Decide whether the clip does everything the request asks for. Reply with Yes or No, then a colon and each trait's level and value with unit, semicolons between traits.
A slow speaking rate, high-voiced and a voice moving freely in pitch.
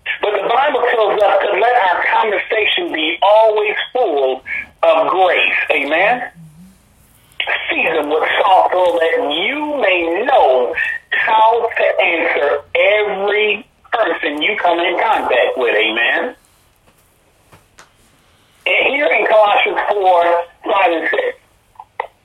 Yes: slow, 115 wpm; high, 215 Hz; wide, 9.0 semitones